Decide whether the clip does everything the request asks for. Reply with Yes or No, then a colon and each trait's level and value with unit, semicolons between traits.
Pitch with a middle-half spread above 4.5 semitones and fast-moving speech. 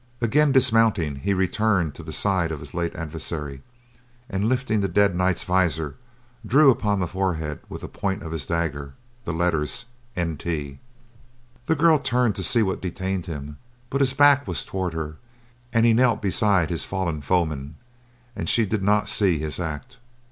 No: average, 5.3 semitones; average, 170 wpm